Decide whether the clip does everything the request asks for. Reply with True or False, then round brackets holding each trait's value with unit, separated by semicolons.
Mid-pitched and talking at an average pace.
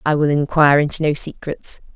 True (150 Hz; 185 wpm)